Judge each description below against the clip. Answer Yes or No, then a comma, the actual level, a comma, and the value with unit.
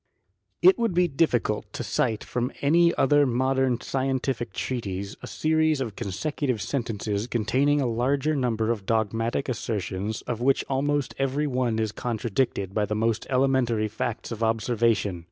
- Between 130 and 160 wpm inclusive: Yes, average, 155 wpm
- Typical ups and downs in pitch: Yes, average, 3.7 semitones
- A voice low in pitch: Yes, low, 120 Hz